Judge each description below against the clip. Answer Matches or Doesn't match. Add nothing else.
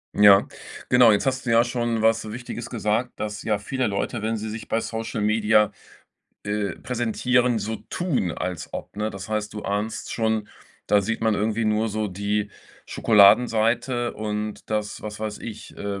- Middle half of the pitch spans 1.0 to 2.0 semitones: Matches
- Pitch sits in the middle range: Doesn't match